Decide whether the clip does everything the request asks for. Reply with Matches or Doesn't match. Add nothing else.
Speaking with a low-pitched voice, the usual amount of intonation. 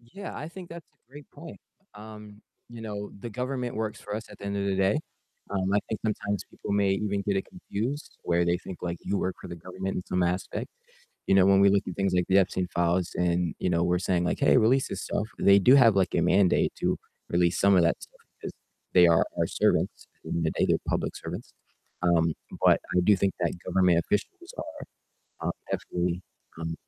Matches